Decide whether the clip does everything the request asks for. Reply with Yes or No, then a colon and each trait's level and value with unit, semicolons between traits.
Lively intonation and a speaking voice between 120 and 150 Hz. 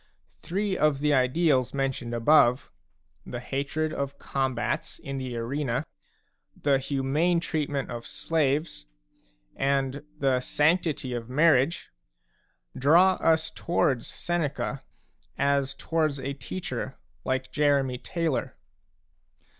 No: average, 3.2 semitones; medium, 140 Hz